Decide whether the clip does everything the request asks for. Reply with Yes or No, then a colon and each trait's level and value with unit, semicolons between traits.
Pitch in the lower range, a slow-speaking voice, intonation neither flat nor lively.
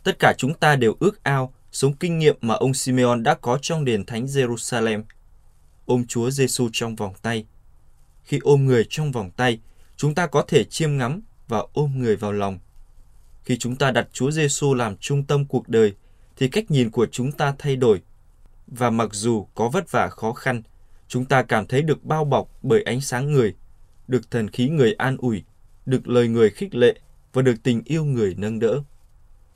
No: low, 120 Hz; average, 200 wpm; average, 4.3 semitones